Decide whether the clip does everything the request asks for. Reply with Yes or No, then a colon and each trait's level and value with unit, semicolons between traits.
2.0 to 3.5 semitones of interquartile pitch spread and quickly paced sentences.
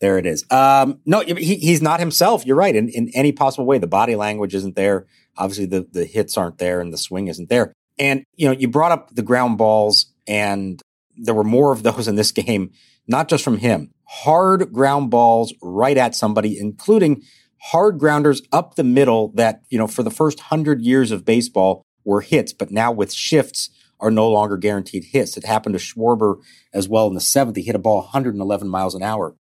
No: average, 5.0 semitones; fast, 210 wpm